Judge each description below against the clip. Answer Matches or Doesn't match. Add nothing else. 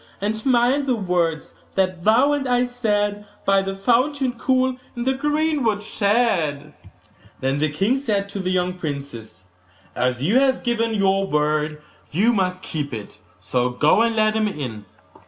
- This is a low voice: Doesn't match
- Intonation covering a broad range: Matches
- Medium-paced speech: Matches